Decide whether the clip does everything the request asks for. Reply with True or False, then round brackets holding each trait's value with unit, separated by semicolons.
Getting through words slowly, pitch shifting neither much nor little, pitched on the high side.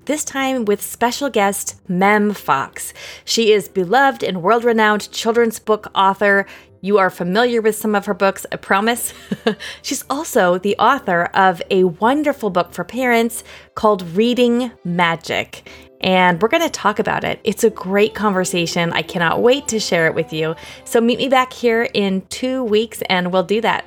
False (175 wpm; 4.0 semitones; 210 Hz)